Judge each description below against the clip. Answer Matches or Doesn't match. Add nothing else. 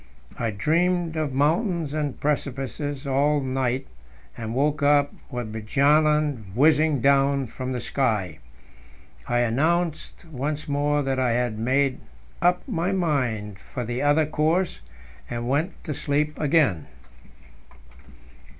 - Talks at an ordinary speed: Doesn't match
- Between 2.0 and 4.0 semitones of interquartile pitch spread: Matches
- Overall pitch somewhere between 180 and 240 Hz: Doesn't match